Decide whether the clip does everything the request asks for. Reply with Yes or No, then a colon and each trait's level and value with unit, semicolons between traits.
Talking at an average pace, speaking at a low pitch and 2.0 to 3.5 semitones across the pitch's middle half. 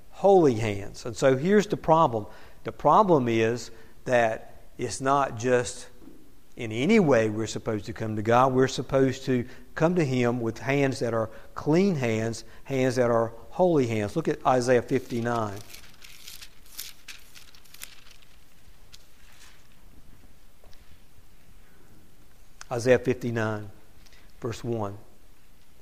No: slow, 110 wpm; low, 120 Hz; average, 3.2 semitones